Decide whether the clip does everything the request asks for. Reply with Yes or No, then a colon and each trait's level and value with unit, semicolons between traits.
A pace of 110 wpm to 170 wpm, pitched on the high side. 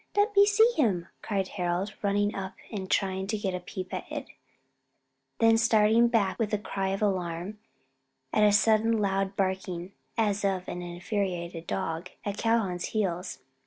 Yes: average, 160 wpm; high, 195 Hz